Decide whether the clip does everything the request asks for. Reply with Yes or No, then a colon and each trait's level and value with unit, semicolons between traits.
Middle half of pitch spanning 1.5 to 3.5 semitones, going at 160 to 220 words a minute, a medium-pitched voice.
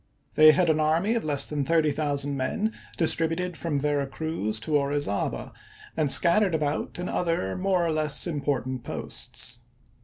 Yes: average, 2.9 semitones; average, 165 wpm; medium, 155 Hz